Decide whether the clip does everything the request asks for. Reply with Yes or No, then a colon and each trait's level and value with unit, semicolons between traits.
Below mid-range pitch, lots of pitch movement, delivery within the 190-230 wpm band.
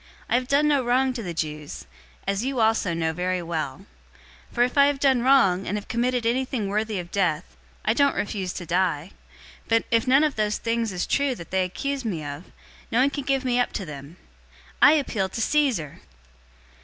No: high, 220 Hz; wide, 6.4 semitones; fast, 205 wpm